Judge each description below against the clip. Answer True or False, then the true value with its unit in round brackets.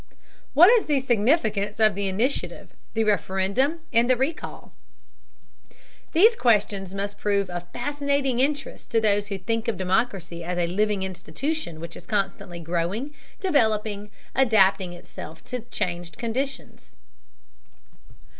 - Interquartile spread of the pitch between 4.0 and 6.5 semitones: True (5.5 semitones)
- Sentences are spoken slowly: True (125 wpm)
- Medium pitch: False (210 Hz)